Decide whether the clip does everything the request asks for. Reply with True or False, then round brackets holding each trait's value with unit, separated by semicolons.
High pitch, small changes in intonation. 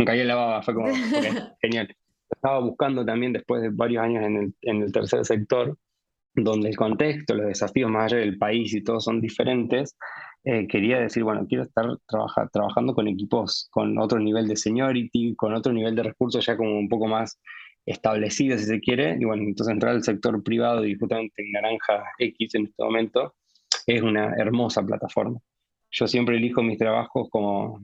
False (115 Hz; 1.9 semitones)